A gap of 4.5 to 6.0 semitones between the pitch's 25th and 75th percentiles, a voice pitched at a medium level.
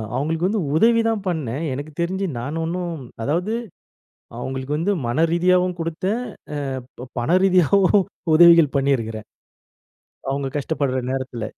Yes: average, 5.2 semitones; medium, 165 Hz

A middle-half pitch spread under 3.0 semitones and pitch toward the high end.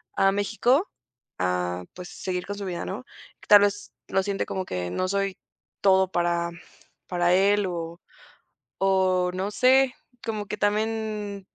Yes: narrow, 2.5 semitones; high, 195 Hz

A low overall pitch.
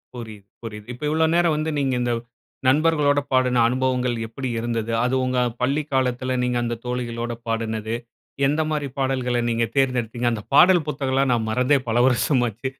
Yes: low, 125 Hz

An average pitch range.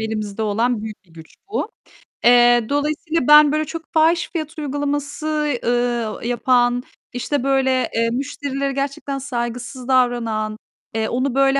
Yes: average, 3.4 semitones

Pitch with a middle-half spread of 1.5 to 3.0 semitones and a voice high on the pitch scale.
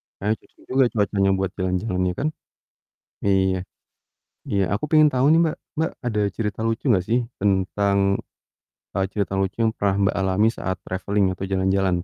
No: average, 2.7 semitones; low, 100 Hz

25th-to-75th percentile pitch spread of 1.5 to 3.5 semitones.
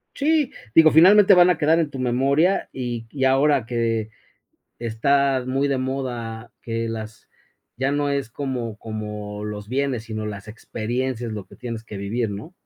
No: average, 4.1 semitones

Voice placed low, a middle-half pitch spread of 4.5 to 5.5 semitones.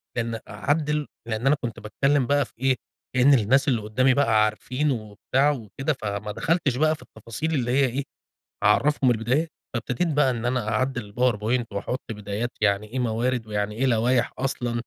No: low, 125 Hz; average, 3.9 semitones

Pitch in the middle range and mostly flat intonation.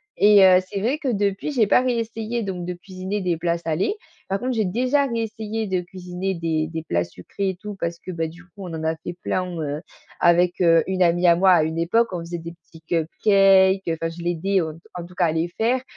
No: medium, 180 Hz; average, 3.5 semitones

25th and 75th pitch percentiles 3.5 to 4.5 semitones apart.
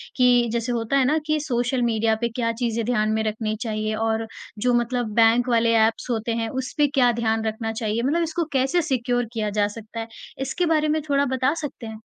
No: average, 2.9 semitones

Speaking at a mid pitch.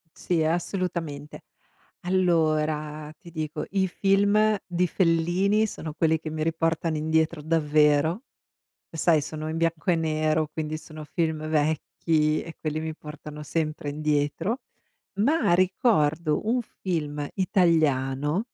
Yes: medium, 160 Hz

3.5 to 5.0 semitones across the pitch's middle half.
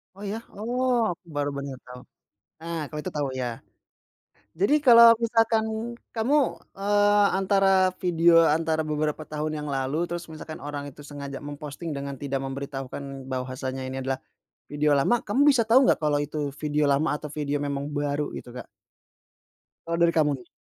No: wide, 5.5 semitones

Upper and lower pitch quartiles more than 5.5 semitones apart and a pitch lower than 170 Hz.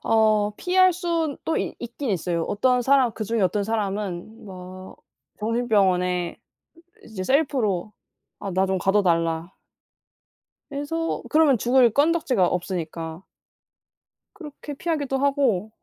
No: wide, 7.0 semitones; high, 220 Hz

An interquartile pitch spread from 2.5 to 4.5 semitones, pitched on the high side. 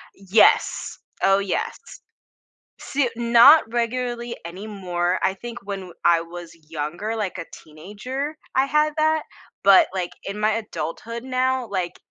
No: average, 5.3 semitones; high, 210 Hz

